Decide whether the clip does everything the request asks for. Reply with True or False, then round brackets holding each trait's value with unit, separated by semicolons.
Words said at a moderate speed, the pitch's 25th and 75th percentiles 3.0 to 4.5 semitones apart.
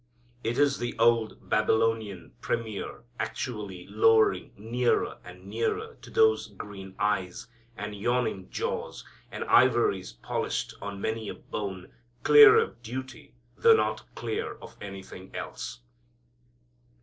False (120 wpm; 3.8 semitones)